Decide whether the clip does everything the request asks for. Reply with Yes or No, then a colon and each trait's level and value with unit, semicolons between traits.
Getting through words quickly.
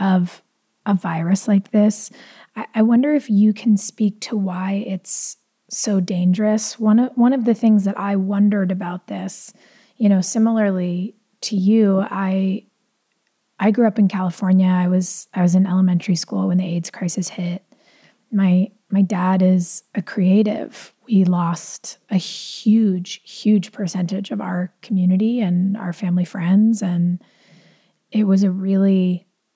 No: average, 150 wpm